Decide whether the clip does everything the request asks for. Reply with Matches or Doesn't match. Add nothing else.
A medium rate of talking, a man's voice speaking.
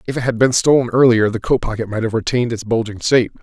Doesn't match